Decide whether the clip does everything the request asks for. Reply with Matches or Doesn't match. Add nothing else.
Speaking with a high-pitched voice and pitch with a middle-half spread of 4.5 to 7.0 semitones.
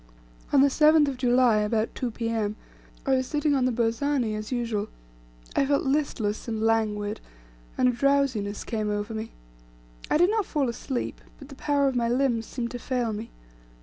Doesn't match